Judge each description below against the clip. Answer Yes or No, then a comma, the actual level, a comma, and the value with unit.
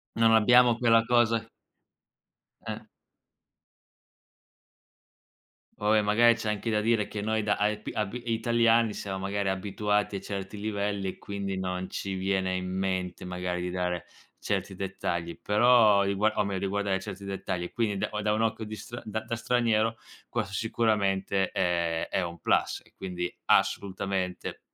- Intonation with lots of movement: No, narrow, 2.6 semitones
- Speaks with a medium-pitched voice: No, low, 100 Hz